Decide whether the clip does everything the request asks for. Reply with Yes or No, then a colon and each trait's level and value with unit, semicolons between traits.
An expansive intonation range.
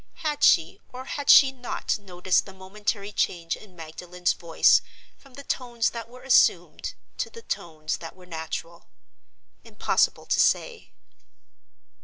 Yes: wide, 6.7 semitones